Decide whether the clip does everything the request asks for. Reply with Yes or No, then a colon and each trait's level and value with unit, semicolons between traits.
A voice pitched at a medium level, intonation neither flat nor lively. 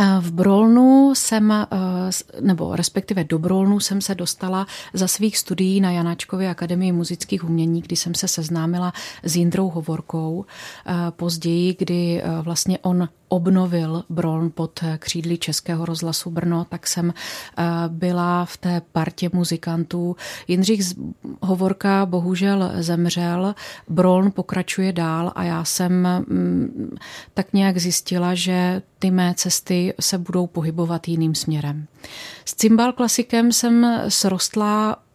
No: medium, 180 Hz; narrow, 2.1 semitones